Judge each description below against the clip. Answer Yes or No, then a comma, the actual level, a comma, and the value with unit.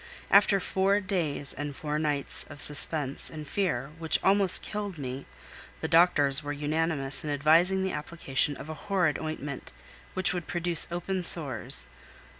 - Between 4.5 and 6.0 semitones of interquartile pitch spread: No, average, 3.9 semitones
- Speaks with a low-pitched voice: No, medium, 155 Hz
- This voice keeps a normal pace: Yes, average, 145 wpm